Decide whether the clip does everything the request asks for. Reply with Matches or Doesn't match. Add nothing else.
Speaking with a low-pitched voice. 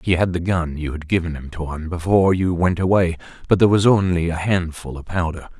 Matches